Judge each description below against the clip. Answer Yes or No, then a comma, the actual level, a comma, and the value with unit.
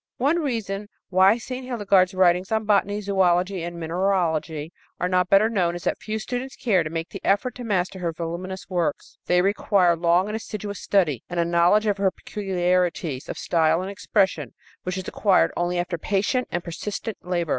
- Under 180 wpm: No, average, 185 wpm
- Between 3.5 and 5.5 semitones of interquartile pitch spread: No, average, 3.0 semitones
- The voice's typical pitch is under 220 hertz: Yes, medium, 185 Hz